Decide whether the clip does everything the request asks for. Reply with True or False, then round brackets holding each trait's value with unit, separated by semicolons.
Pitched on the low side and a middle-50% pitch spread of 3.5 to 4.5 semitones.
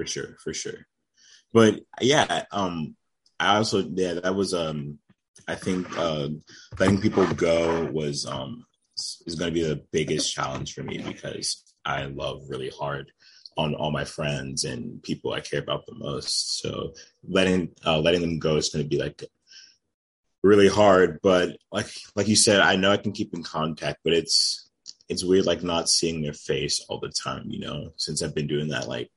True (85 Hz; 3.9 semitones)